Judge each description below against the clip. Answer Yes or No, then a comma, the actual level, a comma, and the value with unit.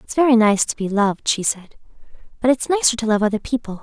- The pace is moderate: No, fast, 235 wpm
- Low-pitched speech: No, high, 230 Hz